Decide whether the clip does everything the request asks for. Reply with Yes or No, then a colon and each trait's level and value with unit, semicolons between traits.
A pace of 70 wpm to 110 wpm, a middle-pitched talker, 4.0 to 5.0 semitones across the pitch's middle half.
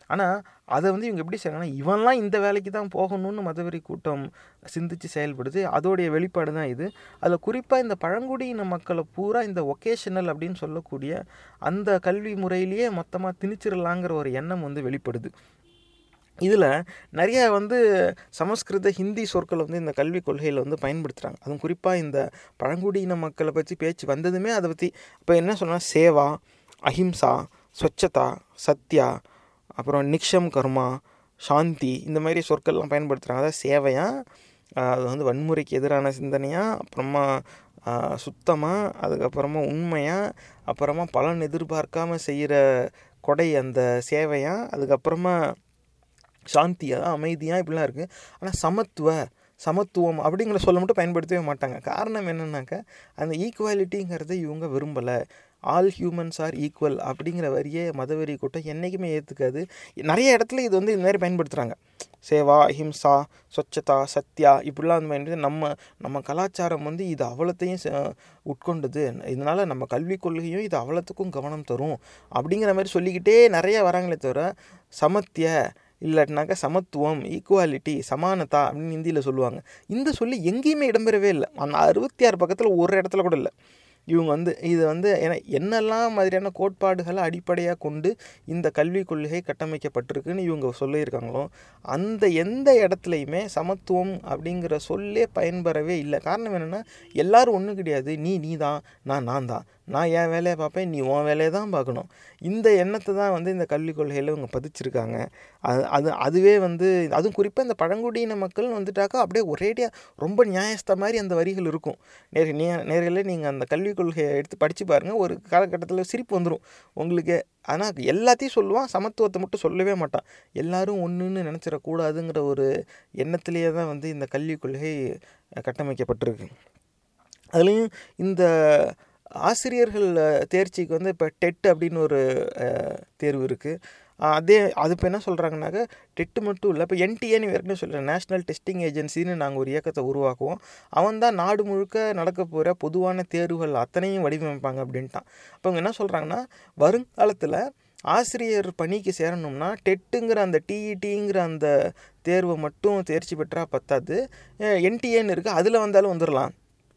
No: fast, 130 wpm; medium, 170 Hz; average, 4.4 semitones